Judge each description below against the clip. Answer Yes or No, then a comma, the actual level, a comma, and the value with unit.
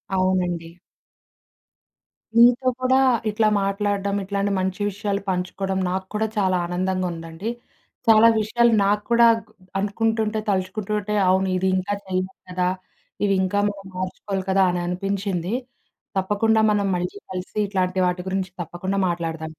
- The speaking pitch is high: Yes, high, 195 Hz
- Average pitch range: No, narrow, 2.1 semitones